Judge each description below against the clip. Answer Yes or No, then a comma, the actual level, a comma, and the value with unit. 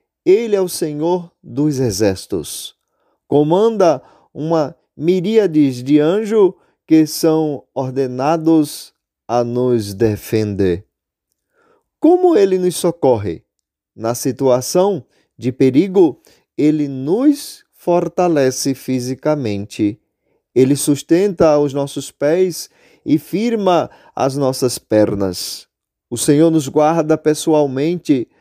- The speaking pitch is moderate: Yes, medium, 150 Hz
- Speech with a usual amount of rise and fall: No, wide, 5.8 semitones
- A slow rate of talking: Yes, slow, 95 wpm